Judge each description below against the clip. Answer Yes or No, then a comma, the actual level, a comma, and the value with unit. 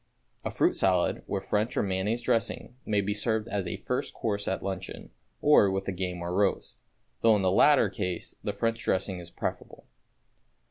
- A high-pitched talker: No, low, 100 Hz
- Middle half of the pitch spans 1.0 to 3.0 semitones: Yes, average, 2.7 semitones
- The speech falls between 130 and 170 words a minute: No, average, 185 wpm